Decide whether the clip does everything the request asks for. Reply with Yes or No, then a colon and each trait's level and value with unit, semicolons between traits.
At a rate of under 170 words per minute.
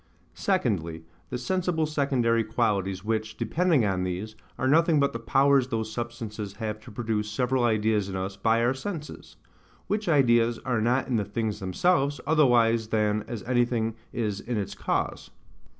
Yes: average, 160 wpm